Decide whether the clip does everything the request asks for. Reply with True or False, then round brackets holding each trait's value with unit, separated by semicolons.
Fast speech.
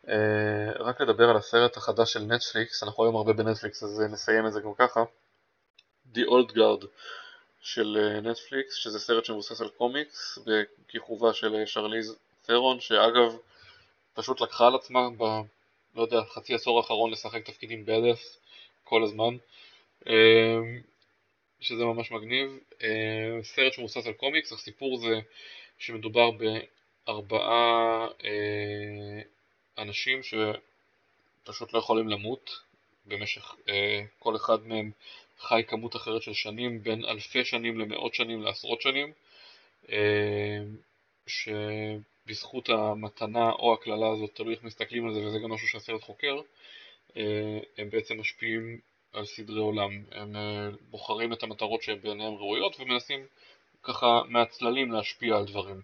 False (125 wpm)